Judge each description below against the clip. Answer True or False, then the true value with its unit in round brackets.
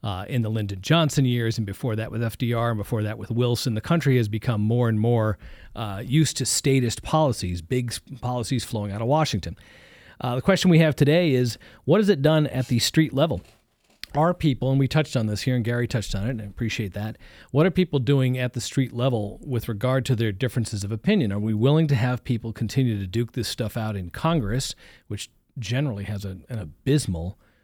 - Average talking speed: False (220 wpm)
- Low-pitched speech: True (120 Hz)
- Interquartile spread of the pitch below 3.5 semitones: False (3.8 semitones)